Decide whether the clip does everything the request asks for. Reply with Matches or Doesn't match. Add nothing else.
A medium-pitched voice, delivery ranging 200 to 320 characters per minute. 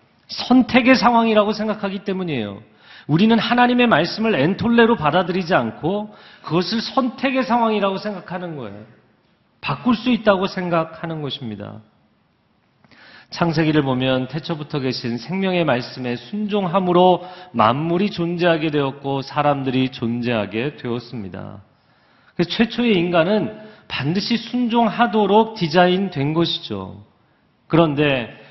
Matches